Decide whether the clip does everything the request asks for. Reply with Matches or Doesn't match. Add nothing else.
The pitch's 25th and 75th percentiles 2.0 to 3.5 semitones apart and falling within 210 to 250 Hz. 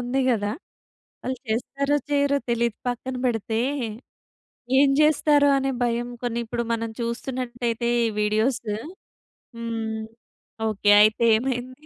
Matches